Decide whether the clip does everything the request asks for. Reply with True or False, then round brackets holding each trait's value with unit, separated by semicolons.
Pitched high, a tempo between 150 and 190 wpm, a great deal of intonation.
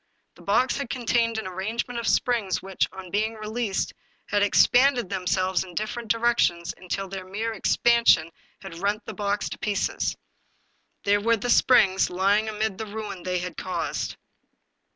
False (205 Hz; 155 wpm; 3.3 semitones)